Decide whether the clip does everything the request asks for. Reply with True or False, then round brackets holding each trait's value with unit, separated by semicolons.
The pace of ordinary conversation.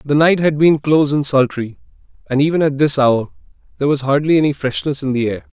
False (215 wpm)